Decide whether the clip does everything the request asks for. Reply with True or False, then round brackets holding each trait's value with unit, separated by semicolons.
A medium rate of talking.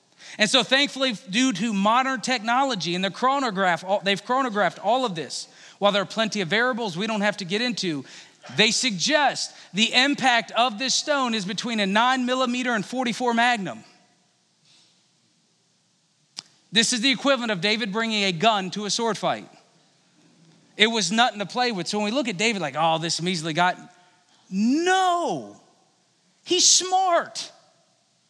True (160 wpm)